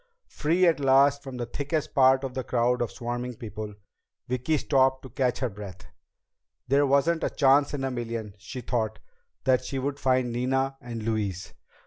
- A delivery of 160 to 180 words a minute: Yes, average, 175 wpm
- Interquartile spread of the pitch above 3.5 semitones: No, average, 2.7 semitones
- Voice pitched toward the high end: No, low, 130 Hz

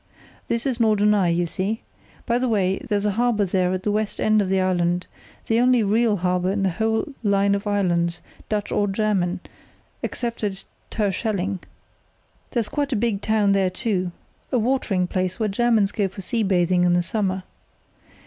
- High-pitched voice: Yes, high, 200 Hz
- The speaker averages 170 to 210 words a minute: Yes, average, 175 wpm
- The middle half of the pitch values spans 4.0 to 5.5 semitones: No, average, 3.0 semitones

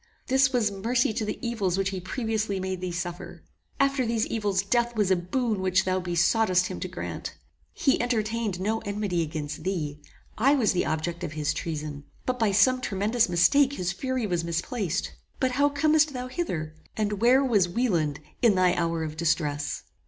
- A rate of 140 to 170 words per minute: No, average, 180 wpm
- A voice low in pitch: No, high, 200 Hz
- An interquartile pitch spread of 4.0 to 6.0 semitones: Yes, wide, 5.5 semitones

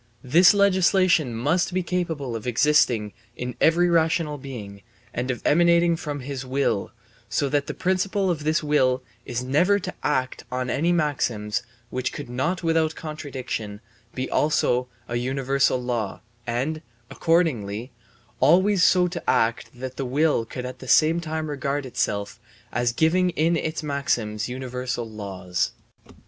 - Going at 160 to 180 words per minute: No, average, 145 wpm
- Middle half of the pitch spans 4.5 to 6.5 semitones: Yes, average, 4.9 semitones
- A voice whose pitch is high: No, medium, 140 Hz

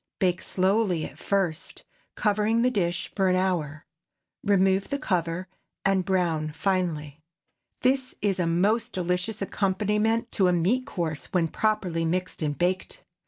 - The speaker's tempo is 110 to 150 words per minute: Yes, average, 140 wpm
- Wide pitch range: No, average, 3.5 semitones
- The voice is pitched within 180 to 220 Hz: Yes, medium, 185 Hz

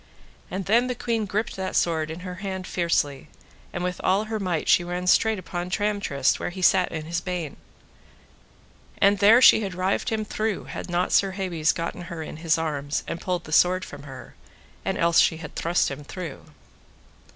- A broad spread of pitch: No, average, 3.2 semitones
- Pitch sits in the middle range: Yes, medium, 180 Hz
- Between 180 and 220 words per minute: Yes, average, 195 wpm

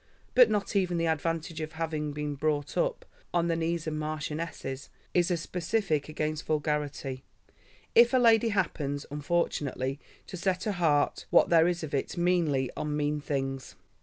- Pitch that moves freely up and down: No, average, 3.0 semitones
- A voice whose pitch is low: No, medium, 155 Hz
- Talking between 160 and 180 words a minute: Yes, average, 165 wpm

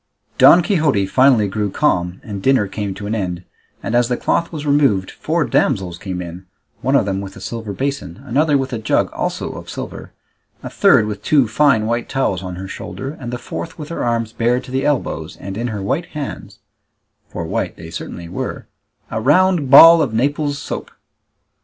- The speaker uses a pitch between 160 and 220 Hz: No, low, 115 Hz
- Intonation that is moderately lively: No, wide, 6.2 semitones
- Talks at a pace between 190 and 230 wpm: Yes, average, 195 wpm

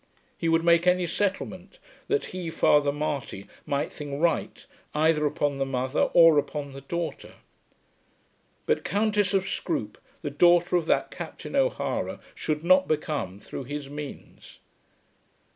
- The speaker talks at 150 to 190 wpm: No, average, 140 wpm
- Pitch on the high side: No, medium, 155 Hz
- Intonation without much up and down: No, average, 3.6 semitones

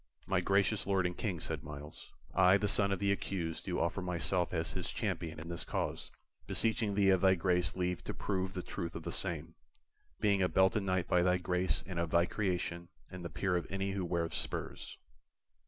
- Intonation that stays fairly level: Yes, narrow, 2.2 semitones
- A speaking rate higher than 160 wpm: Yes, fast, 205 wpm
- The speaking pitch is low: Yes, very low, 90 Hz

